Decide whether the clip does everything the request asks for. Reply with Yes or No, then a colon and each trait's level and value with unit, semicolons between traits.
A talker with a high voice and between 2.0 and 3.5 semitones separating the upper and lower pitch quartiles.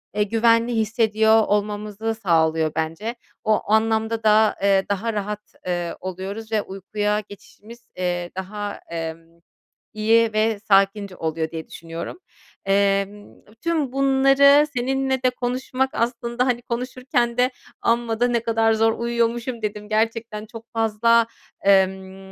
Yes: high, 220 Hz; average, 3.0 semitones